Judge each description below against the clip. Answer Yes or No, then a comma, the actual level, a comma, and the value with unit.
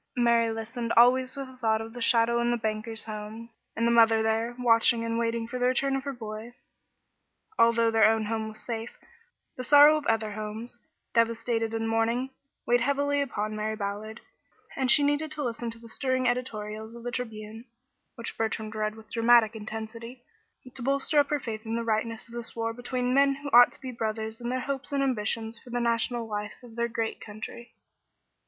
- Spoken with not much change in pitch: Yes, narrow, 1.9 semitones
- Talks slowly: No, average, 200 wpm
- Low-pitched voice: No, high, 230 Hz